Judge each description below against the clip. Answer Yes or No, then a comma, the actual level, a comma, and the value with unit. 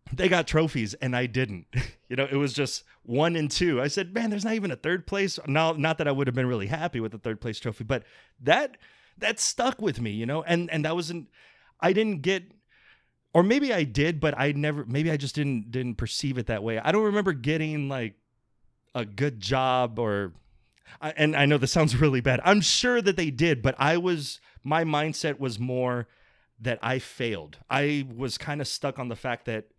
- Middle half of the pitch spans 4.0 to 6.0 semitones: Yes, average, 4.7 semitones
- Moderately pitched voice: Yes, medium, 145 Hz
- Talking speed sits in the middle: No, fast, 220 wpm